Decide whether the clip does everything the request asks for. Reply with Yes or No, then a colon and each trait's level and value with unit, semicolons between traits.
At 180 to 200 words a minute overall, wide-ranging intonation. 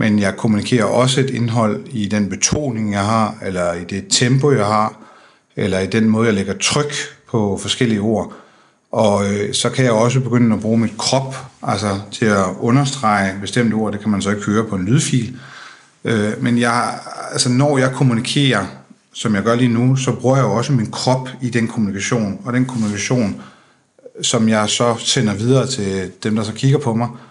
No: average, 195 wpm; average, 3.4 semitones